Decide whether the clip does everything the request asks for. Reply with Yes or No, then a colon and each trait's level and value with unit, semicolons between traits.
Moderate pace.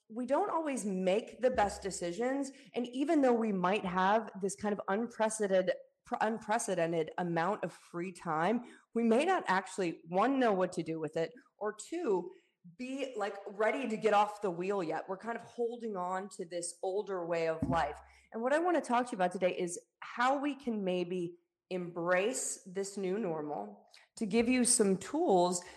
Yes: average, 185 wpm